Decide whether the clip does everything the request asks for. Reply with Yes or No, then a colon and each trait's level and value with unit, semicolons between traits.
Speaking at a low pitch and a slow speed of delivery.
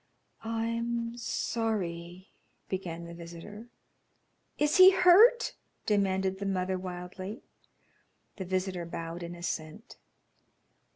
No: high, 190 Hz; slow, 100 wpm